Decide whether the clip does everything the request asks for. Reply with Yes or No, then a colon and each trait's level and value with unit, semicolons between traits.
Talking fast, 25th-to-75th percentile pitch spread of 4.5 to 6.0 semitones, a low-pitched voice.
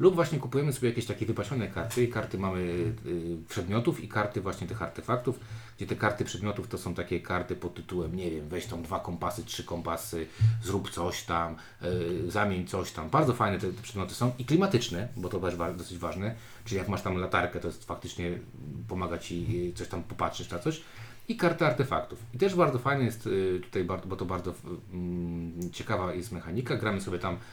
Yes: fast, 185 wpm; average, 5.1 semitones; very low, 95 Hz